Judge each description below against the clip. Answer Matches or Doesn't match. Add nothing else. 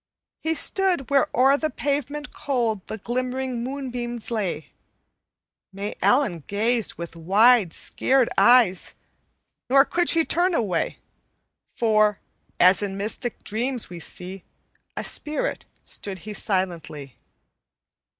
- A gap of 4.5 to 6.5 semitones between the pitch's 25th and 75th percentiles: Matches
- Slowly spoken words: Matches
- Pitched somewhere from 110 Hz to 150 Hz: Doesn't match